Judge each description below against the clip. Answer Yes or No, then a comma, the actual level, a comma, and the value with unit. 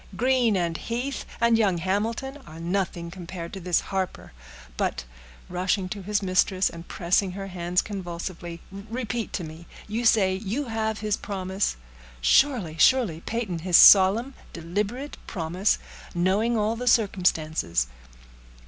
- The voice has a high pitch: Yes, high, 195 Hz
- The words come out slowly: Yes, slow, 130 wpm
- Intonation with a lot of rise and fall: No, average, 4.3 semitones